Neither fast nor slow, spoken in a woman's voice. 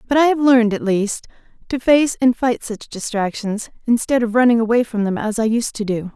No: fast, 225 wpm; female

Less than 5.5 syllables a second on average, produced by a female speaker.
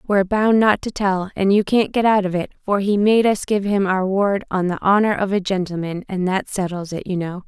Yes: 5.3 syllables/s; female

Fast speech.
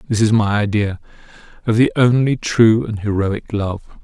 No: average, 165 wpm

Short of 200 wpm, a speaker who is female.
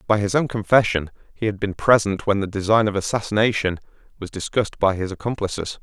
No: average, 185 wpm; male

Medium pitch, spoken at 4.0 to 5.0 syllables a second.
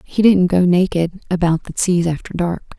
No: medium, 180 Hz; 5.2 syllables/s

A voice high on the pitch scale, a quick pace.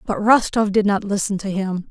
Yes: high, 200 Hz; fast, 220 wpm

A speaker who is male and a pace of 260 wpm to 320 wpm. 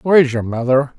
No: male; fast, 245 wpm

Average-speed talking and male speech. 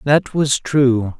Yes: average, 150 wpm; male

